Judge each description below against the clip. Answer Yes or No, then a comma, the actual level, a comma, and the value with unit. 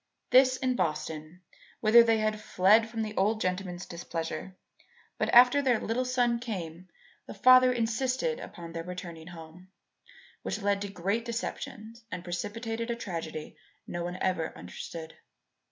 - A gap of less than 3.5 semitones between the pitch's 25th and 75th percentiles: No, average, 5.2 semitones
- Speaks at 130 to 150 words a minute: Yes, average, 145 wpm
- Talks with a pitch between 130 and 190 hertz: No, high, 205 Hz